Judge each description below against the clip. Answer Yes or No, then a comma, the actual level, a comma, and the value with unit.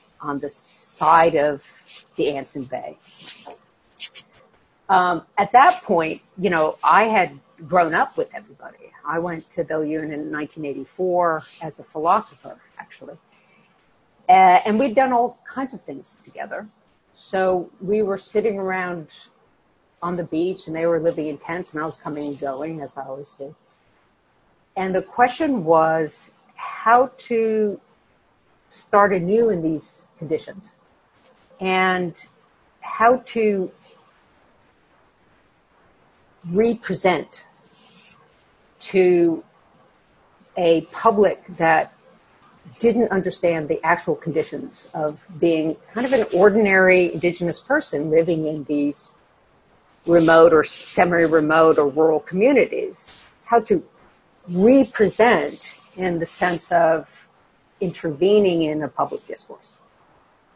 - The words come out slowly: Yes, slow, 115 wpm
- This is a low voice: No, medium, 175 Hz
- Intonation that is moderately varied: Yes, average, 4.9 semitones